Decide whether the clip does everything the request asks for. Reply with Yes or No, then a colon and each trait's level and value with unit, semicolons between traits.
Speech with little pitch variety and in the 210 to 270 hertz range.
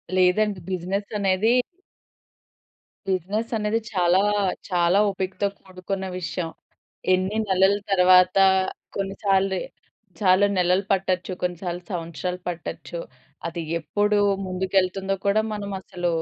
No: narrow, 1.5 semitones; medium, 185 Hz